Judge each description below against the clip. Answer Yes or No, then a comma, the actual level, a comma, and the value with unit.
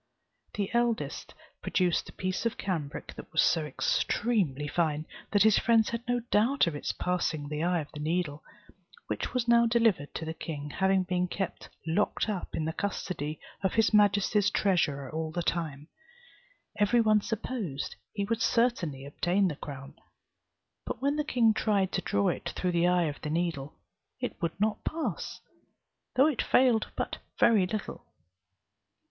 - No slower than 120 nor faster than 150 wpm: No, average, 165 wpm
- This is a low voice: No, medium, 185 Hz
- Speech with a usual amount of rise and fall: No, wide, 5.7 semitones